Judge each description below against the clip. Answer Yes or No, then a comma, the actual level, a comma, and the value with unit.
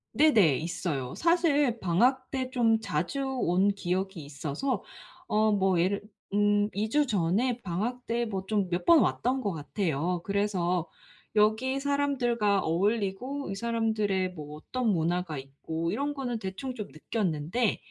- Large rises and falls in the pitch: Yes, wide, 5.9 semitones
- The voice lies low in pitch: No, high, 205 Hz